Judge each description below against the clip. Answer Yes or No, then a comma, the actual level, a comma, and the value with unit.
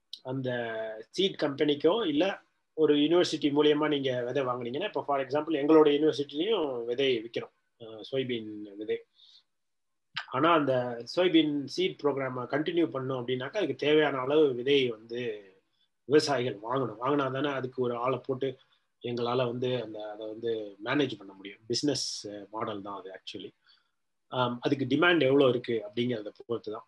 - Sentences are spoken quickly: Yes, fast, 135 wpm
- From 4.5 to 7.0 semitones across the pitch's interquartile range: No, average, 4.0 semitones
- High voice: No, low, 130 Hz